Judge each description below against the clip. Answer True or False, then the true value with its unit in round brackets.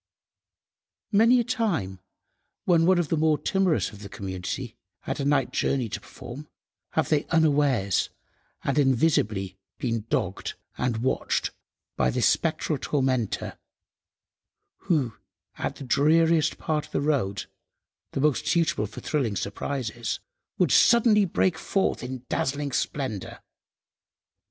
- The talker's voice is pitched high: False (140 Hz)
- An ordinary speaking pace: False (120 wpm)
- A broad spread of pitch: True (6.0 semitones)